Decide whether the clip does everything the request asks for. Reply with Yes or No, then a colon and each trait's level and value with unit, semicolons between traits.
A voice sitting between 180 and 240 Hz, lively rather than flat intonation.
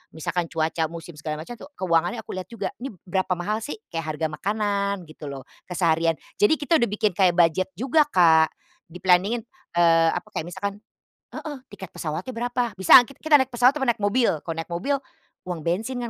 Yes: medium, 185 Hz; wide, 5.8 semitones